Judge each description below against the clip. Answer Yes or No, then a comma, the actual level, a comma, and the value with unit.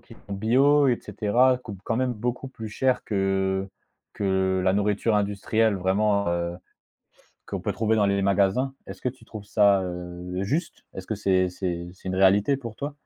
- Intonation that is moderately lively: Yes, average, 3.5 semitones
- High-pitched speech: No, low, 100 Hz